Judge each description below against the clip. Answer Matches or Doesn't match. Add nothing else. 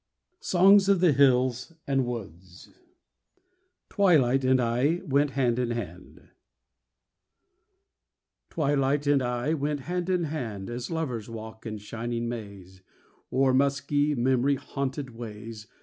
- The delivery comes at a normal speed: Doesn't match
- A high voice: Doesn't match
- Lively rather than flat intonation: Doesn't match